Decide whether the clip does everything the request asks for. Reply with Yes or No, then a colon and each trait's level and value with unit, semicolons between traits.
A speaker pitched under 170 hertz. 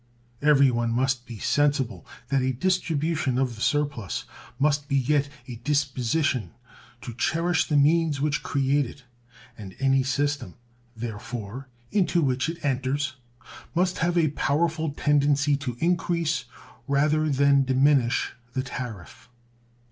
Yes: medium, 140 Hz